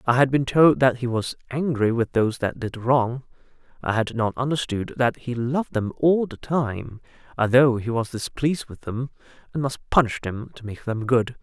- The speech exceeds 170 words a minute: Yes, average, 200 wpm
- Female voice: No, male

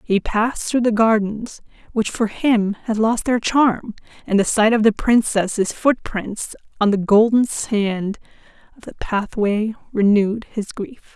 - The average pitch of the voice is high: Yes, high, 215 Hz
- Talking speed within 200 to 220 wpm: No, average, 155 wpm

